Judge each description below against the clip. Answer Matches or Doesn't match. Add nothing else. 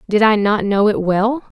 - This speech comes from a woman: Matches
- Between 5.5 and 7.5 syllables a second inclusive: Doesn't match